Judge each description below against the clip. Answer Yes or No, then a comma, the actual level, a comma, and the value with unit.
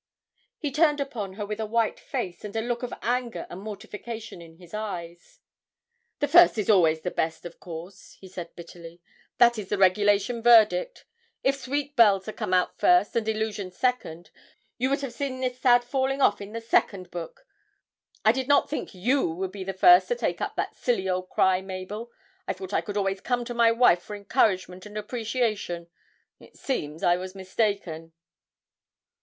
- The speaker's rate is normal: Yes, average, 185 wpm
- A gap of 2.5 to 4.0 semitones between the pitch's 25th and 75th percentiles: No, average, 4.7 semitones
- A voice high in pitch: Yes, high, 210 Hz